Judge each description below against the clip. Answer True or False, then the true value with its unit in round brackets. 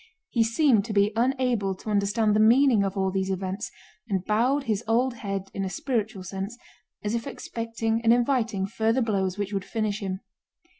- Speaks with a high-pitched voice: True (215 Hz)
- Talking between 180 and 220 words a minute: True (185 wpm)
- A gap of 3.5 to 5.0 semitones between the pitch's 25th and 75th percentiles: False (2.9 semitones)